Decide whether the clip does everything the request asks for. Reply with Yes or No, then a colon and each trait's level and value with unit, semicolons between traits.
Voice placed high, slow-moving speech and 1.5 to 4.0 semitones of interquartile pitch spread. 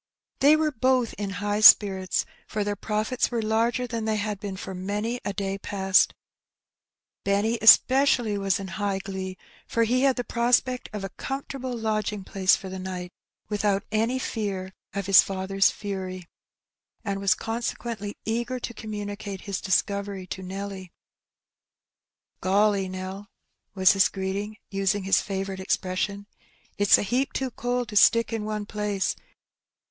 No: high, 205 Hz; average, 150 wpm; average, 2.7 semitones